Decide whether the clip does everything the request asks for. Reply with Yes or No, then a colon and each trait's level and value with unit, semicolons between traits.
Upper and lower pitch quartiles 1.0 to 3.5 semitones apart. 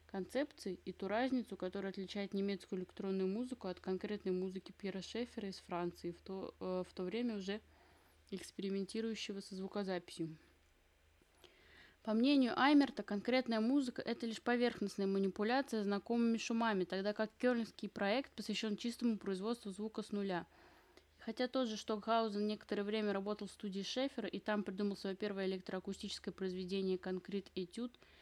Yes: average, 2.9 semitones